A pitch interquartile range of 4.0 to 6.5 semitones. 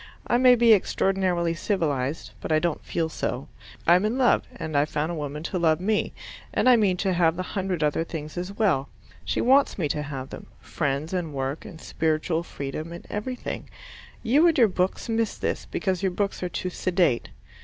Yes: average, 4.6 semitones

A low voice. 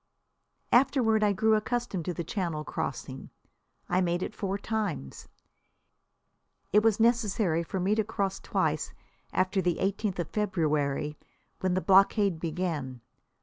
No: high, 190 Hz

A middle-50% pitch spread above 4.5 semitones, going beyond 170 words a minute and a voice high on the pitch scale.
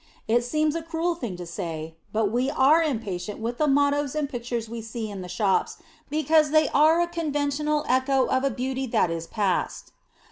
Yes: wide, 5.6 semitones; average, 190 wpm; very high, 260 Hz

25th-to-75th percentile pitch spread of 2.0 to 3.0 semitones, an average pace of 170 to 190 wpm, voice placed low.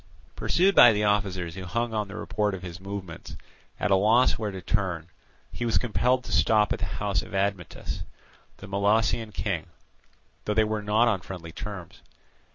Yes: narrow, 2.5 semitones; average, 180 wpm; low, 105 Hz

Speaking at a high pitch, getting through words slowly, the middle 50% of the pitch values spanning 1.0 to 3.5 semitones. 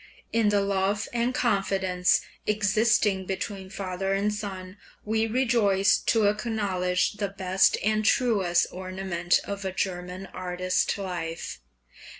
Yes: high, 195 Hz; slow, 120 wpm; narrow, 2.4 semitones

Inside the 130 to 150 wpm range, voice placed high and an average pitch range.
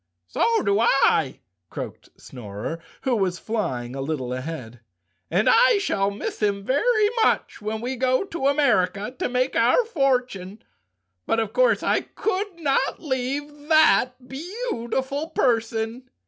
No: average, 140 wpm; high, 245 Hz; wide, 6.7 semitones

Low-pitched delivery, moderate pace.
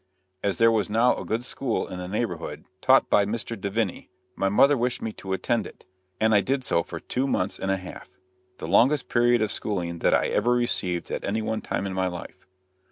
No: low, 110 Hz; fast, 220 wpm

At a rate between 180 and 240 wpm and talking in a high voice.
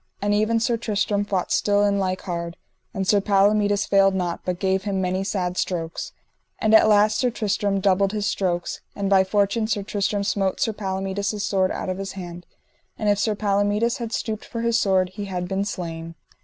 Yes: average, 200 wpm; high, 200 Hz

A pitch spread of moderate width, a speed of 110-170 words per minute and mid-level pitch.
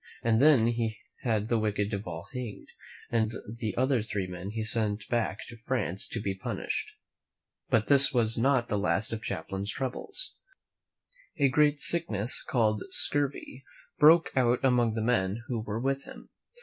No: average, 3.6 semitones; average, 155 wpm; low, 115 Hz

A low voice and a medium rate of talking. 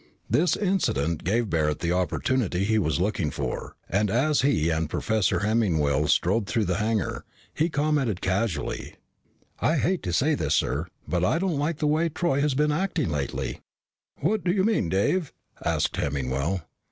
Yes: low, 110 Hz; average, 165 wpm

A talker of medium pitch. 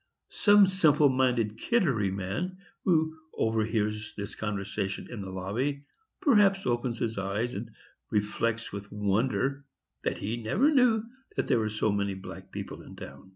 No: low, 115 Hz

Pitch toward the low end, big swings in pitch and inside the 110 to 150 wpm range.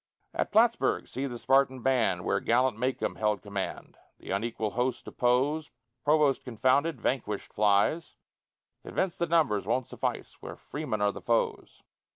No: low, 125 Hz; average, 4.9 semitones; average, 145 wpm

